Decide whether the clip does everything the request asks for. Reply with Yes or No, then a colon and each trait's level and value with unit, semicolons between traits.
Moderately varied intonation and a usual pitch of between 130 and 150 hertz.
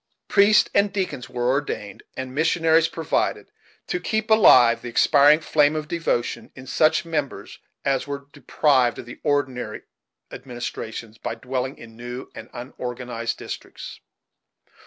Yes: average, 4.5 semitones; low, 135 Hz